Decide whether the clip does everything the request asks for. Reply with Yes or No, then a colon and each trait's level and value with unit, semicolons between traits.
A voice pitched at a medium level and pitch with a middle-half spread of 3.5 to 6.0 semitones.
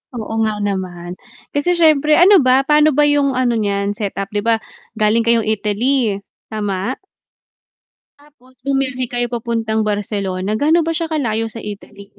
No: high, 230 Hz; average, 5.2 semitones